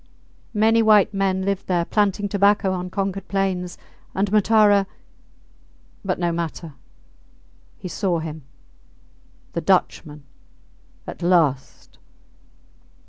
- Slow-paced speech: Yes, slow, 100 wpm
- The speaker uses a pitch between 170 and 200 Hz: Yes, high, 190 Hz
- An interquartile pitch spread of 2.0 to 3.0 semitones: Yes, average, 2.7 semitones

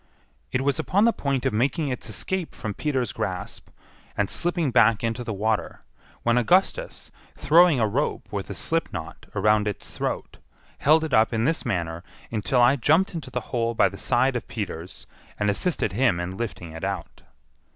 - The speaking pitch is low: Yes, low, 120 Hz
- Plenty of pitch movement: Yes, wide, 5.8 semitones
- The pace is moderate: Yes, average, 180 wpm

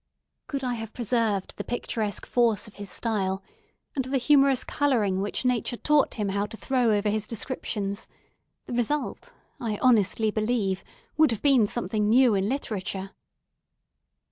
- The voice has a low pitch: No, high, 225 Hz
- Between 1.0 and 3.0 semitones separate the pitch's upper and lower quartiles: No, average, 3.6 semitones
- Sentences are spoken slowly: No, average, 150 wpm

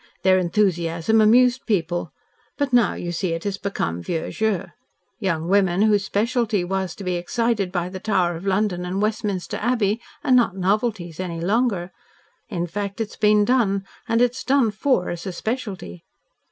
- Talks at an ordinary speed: Yes, average, 165 wpm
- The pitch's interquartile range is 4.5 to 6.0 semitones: No, average, 3.8 semitones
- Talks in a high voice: Yes, high, 200 Hz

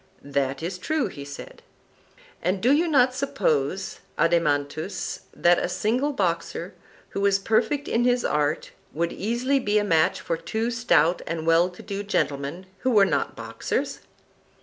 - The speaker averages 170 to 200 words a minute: No, average, 155 wpm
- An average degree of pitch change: No, wide, 6.3 semitones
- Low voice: No, high, 190 Hz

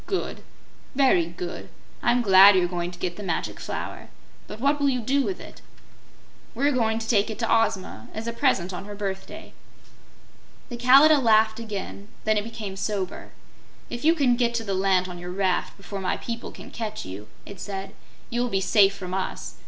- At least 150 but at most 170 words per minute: No, average, 190 wpm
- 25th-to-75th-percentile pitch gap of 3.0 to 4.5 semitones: Yes, average, 3.9 semitones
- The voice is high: Yes, high, 210 Hz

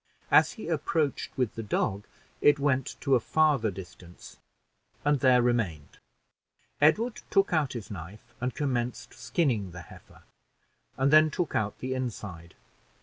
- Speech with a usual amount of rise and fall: No, wide, 6.1 semitones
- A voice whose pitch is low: Yes, low, 125 Hz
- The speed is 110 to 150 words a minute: Yes, average, 145 wpm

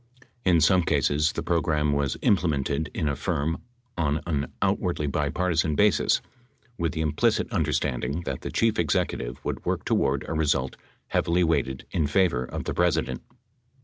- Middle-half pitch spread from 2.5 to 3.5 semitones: Yes, average, 3.1 semitones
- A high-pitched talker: No, very low, 75 Hz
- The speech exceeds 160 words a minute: No, average, 155 wpm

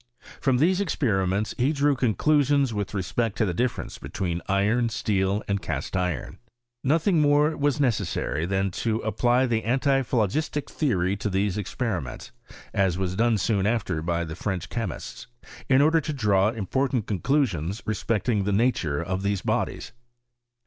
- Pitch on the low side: Yes, low, 110 Hz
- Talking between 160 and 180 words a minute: No, average, 150 wpm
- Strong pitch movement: Yes, wide, 5.7 semitones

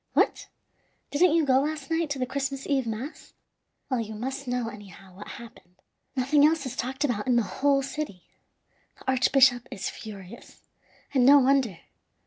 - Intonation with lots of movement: No, average, 3.6 semitones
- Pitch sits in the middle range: No, very high, 260 Hz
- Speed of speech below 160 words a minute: No, average, 165 wpm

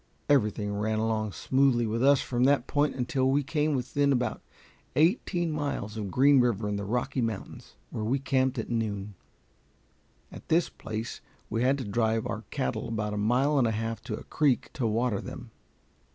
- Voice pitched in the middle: No, low, 120 Hz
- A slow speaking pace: No, average, 180 wpm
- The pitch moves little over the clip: No, average, 4.1 semitones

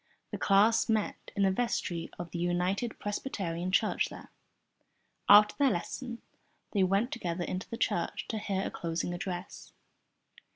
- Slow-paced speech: No, average, 150 wpm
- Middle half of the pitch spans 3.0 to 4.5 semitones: Yes, average, 3.7 semitones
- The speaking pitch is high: Yes, high, 195 Hz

